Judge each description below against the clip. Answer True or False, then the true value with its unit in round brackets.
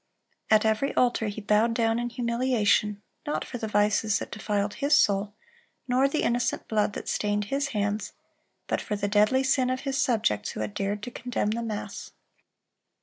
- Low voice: False (220 Hz)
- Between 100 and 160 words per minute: False (185 wpm)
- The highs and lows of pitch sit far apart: False (3.1 semitones)